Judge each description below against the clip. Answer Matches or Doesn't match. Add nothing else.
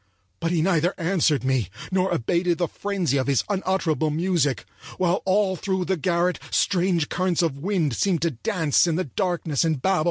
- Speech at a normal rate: Matches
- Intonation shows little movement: Doesn't match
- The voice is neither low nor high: Matches